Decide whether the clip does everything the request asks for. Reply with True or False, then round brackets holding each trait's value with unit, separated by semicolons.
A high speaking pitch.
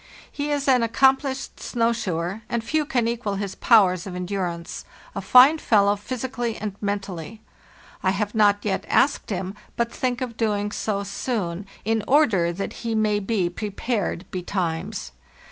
True (210 Hz)